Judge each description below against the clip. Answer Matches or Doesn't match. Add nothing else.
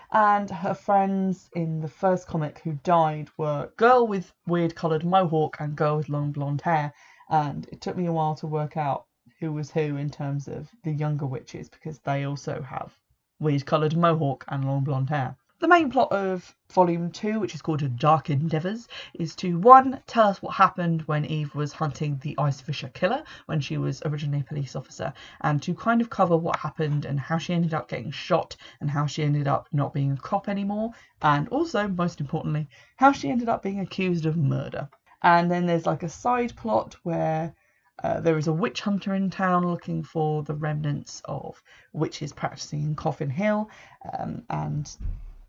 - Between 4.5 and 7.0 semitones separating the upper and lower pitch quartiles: Doesn't match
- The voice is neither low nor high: Matches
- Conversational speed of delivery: Matches